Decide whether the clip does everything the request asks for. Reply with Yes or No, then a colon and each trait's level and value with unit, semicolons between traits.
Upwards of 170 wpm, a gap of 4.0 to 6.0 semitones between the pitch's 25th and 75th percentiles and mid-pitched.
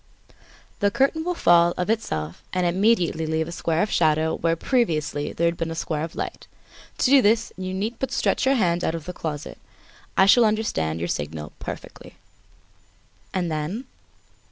Yes: average, 180 wpm; wide, 5.5 semitones; medium, 175 Hz